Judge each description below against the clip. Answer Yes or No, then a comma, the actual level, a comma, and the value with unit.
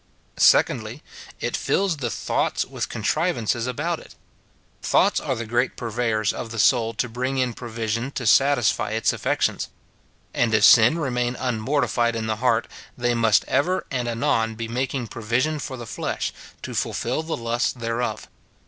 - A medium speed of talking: Yes, average, 160 wpm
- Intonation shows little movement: Yes, narrow, 2.3 semitones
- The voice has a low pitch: Yes, low, 120 Hz